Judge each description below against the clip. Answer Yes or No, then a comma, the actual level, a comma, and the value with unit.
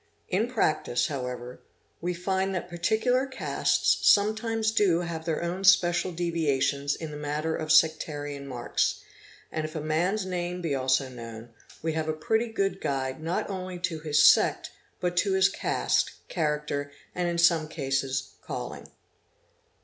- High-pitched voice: No, medium, 165 Hz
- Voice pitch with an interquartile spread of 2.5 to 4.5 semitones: Yes, average, 4.2 semitones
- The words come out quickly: No, average, 150 wpm